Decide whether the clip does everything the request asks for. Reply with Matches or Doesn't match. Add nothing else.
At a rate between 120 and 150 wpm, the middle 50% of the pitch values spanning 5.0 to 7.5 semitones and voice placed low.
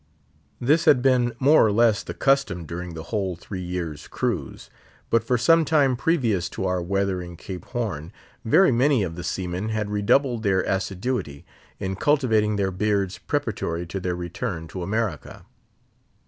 Doesn't match